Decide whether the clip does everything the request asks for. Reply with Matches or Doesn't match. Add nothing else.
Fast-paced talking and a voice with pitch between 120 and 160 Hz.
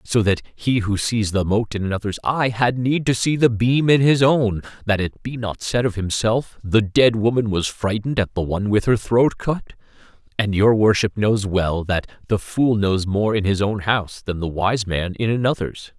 Doesn't match